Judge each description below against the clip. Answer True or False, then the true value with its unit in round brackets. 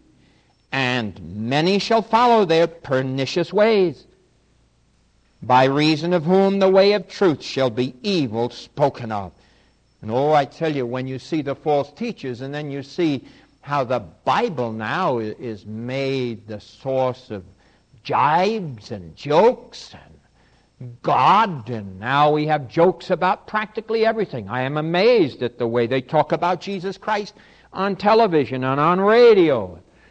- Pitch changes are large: True (7.4 semitones)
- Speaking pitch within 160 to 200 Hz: False (140 Hz)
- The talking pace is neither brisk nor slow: True (145 wpm)